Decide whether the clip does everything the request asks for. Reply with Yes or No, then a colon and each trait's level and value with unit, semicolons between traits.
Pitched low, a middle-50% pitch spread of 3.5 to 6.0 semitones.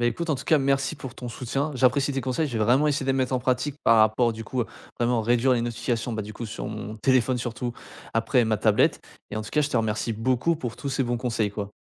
No: low, 120 Hz; average, 2.9 semitones